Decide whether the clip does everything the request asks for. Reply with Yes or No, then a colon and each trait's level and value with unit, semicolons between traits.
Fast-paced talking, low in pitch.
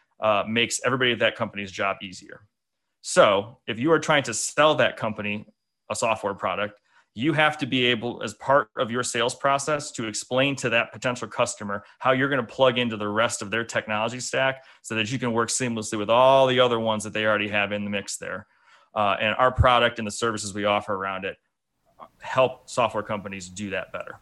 Yes: fast, 210 wpm; low, 115 Hz